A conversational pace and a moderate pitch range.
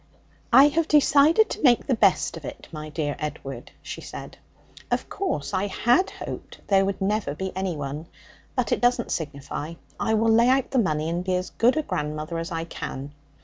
No: average, 190 wpm; wide, 8.0 semitones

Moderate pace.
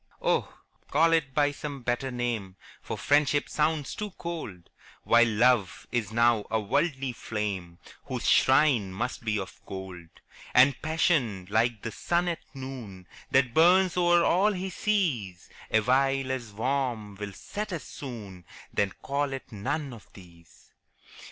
Yes: average, 145 wpm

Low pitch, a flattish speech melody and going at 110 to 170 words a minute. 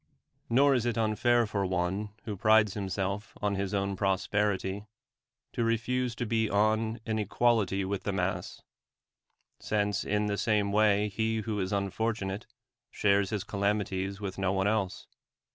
Yes: low, 105 Hz; narrow, 2.1 semitones; average, 150 wpm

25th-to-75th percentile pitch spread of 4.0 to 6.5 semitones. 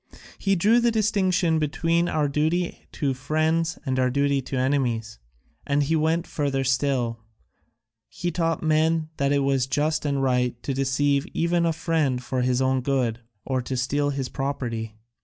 No: average, 3.6 semitones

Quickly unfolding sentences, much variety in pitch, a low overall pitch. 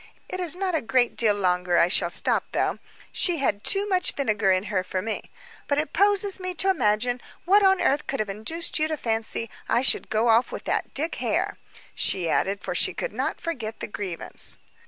No: fast, 210 wpm; wide, 8.7 semitones; high, 245 Hz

